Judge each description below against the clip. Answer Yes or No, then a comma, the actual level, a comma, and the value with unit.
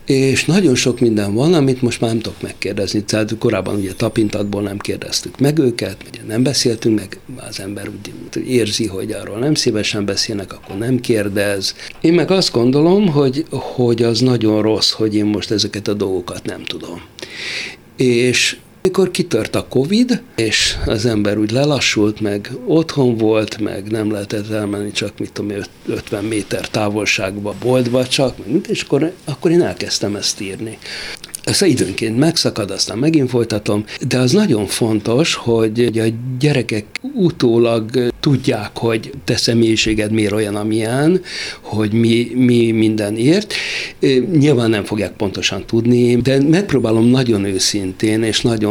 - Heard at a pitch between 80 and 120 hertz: Yes, low, 115 Hz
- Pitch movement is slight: No, average, 3.7 semitones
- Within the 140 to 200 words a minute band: Yes, average, 150 wpm